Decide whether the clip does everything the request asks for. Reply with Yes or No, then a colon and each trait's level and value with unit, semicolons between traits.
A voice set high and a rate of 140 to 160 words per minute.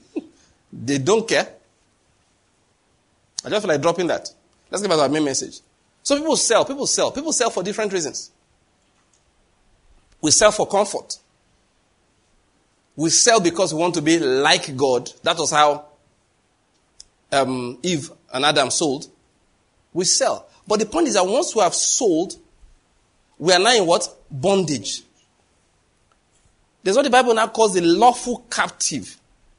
No: medium, 180 Hz; average, 145 wpm